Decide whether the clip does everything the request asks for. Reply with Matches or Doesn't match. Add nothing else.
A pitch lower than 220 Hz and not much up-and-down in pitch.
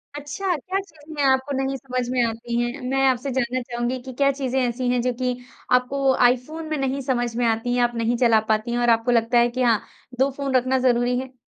Doesn't match